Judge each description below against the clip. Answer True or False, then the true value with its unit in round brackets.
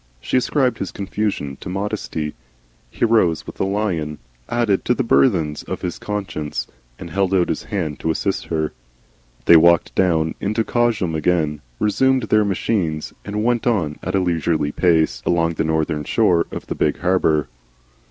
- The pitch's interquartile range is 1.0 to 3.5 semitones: False (4.8 semitones)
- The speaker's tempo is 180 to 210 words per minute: False (165 wpm)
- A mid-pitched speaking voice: False (90 Hz)